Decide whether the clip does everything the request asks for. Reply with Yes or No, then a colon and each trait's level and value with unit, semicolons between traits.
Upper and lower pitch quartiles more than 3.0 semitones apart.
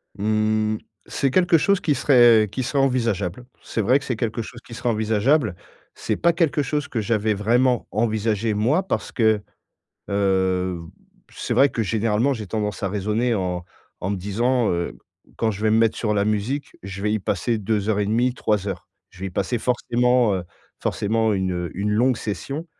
Yes: average, 3.4 semitones